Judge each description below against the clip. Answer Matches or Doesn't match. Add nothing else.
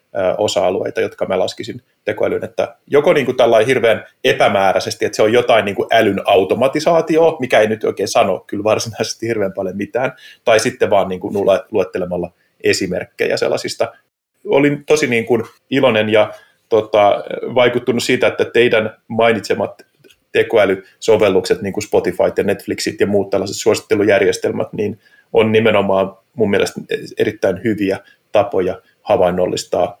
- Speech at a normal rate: Matches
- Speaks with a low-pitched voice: Doesn't match